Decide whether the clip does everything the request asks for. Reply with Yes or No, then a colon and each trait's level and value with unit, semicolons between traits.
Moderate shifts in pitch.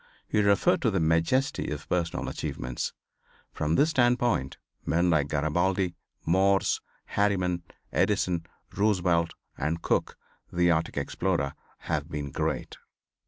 Yes: average, 3.8 semitones